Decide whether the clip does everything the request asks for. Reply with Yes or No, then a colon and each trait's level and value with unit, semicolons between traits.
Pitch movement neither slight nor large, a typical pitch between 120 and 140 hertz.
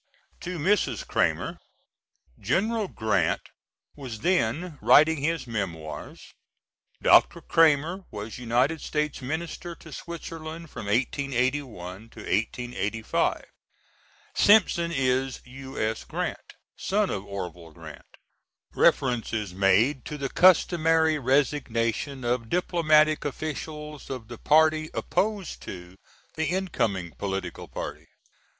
No: wide, 6.4 semitones; low, 135 Hz